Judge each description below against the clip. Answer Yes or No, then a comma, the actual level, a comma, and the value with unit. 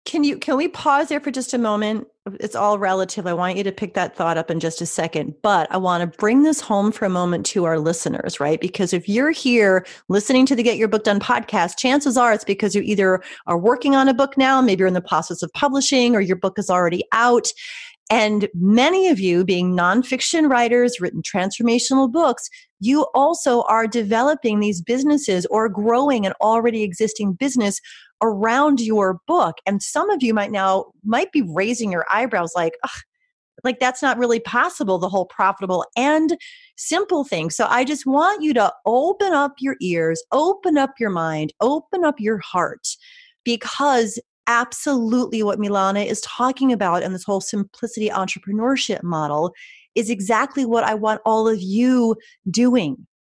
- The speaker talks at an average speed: Yes, average, 185 wpm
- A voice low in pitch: No, high, 225 Hz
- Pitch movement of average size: No, wide, 5.8 semitones